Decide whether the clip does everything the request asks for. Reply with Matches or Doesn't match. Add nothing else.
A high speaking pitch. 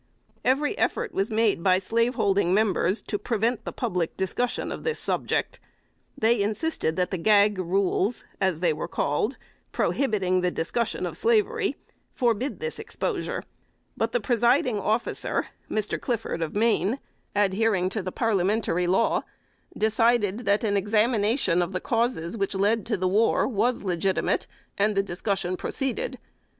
Matches